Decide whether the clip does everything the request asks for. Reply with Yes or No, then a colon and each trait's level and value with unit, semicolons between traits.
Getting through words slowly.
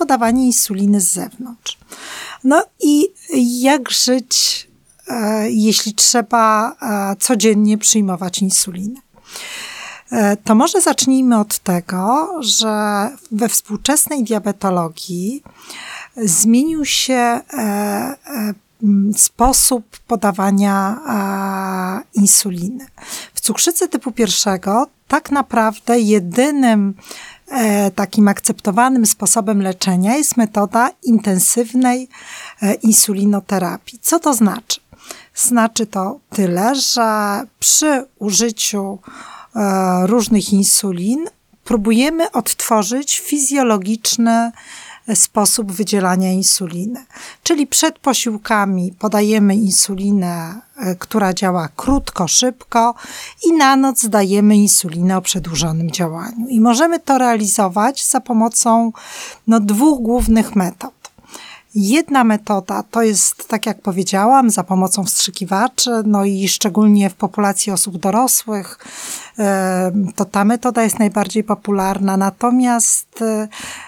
Yes: slow, 90 wpm